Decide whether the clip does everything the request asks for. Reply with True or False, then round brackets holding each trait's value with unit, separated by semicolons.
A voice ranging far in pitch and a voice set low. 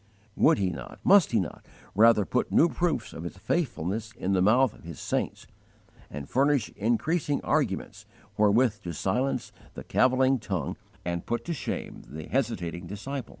True (6.1 semitones; 110 Hz)